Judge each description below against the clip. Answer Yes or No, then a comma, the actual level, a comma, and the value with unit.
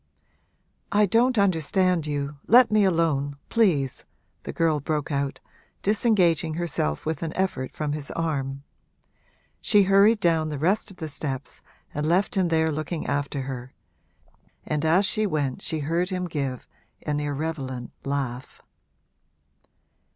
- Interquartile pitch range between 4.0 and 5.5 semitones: Yes, average, 4.6 semitones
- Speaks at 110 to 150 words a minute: Yes, slow, 135 wpm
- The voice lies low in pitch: No, medium, 160 Hz